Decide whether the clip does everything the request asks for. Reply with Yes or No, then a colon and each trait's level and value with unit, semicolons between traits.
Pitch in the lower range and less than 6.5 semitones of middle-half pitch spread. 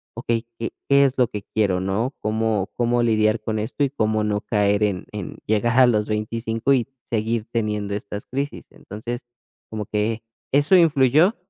Yes: low, 110 Hz; narrow, 2.5 semitones